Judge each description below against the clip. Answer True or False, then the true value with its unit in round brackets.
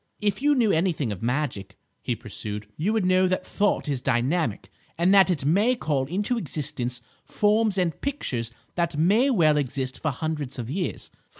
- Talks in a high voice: False (160 Hz)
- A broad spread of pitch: True (7.1 semitones)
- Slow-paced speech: False (175 wpm)